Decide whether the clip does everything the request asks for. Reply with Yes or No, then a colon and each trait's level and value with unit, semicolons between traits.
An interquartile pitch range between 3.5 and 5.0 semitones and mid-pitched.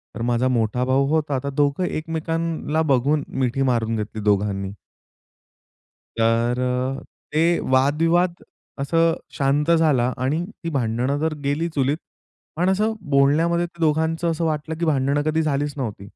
Yes: average, 4.2 semitones; medium, 145 Hz